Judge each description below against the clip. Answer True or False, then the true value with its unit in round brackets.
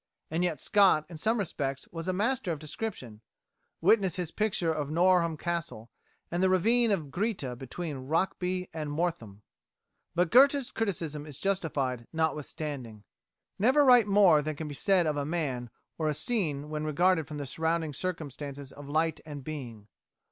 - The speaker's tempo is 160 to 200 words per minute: True (165 wpm)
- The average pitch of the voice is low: False (160 Hz)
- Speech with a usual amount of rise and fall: True (4.4 semitones)